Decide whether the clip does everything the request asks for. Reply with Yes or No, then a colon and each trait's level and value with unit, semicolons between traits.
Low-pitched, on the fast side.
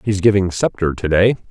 No: very low, 95 Hz; average, 160 wpm